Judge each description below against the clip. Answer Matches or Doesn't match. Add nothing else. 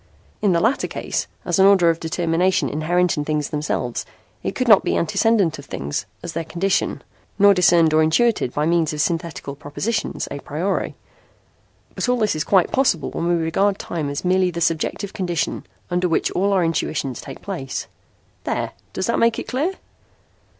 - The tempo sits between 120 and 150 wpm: Doesn't match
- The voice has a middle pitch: Matches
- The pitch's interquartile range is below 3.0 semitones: Doesn't match